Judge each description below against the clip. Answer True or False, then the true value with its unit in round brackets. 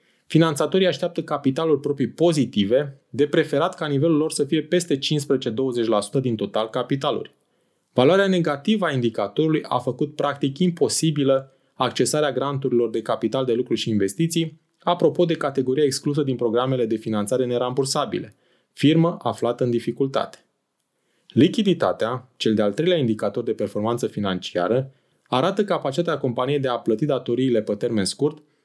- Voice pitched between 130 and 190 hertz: True (140 Hz)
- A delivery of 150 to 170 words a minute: False (135 wpm)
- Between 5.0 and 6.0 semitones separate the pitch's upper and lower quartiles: False (4.2 semitones)